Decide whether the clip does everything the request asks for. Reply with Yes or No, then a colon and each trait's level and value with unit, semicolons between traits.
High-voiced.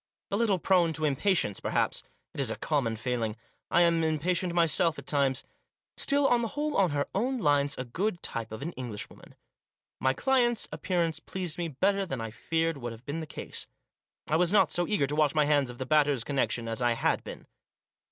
No: medium, 155 Hz